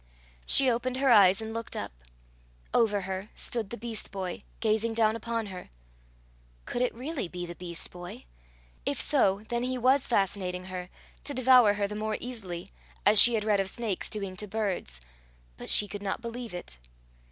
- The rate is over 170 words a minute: Yes, average, 180 wpm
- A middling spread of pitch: Yes, average, 3.9 semitones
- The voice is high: Yes, high, 215 Hz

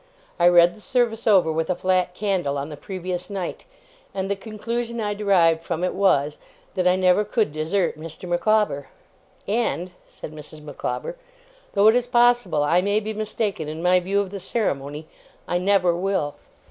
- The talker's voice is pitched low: No, medium, 185 Hz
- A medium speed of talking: Yes, average, 175 wpm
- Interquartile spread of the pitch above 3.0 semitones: Yes, average, 4.1 semitones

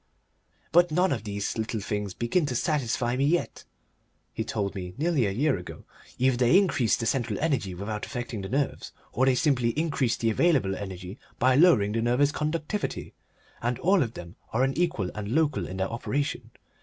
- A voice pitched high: No, low, 120 Hz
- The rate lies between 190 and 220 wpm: No, average, 180 wpm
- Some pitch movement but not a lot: No, wide, 5.9 semitones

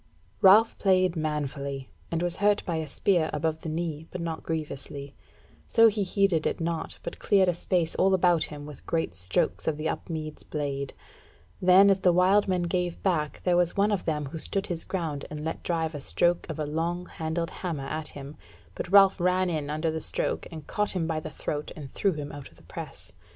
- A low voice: No, medium, 165 Hz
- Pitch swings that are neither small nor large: Yes, average, 3.2 semitones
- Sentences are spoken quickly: Yes, fast, 210 wpm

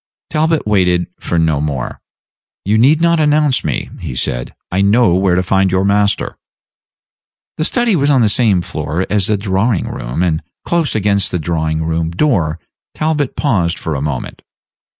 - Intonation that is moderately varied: No, wide, 7.2 semitones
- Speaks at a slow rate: No, average, 170 wpm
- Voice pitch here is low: Yes, very low, 95 Hz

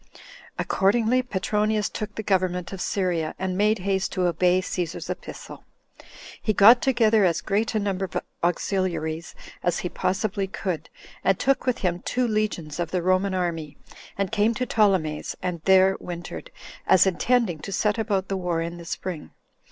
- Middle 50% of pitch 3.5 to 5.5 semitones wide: No, average, 3.1 semitones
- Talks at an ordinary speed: Yes, average, 165 wpm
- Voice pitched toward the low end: No, high, 190 Hz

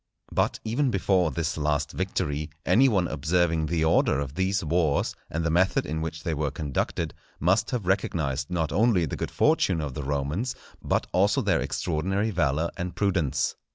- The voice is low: Yes, very low, 85 Hz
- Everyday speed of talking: Yes, average, 175 wpm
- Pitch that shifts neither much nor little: Yes, average, 4.0 semitones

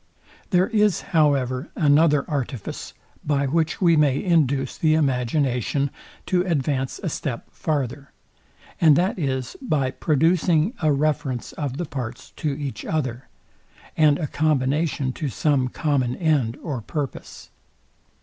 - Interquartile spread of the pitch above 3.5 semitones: No, average, 3.2 semitones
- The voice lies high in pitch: No, medium, 145 Hz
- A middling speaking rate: No, slow, 130 wpm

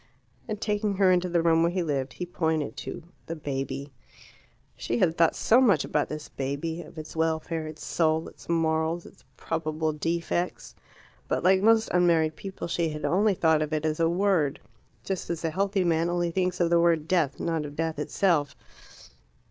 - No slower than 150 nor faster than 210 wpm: Yes, average, 190 wpm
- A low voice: No, medium, 165 Hz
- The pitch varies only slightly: Yes, narrow, 2.3 semitones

